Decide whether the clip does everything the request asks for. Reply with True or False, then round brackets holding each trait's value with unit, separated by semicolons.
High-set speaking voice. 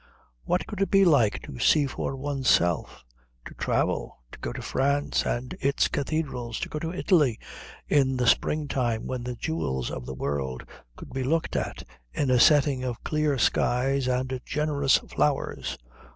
False (135 Hz)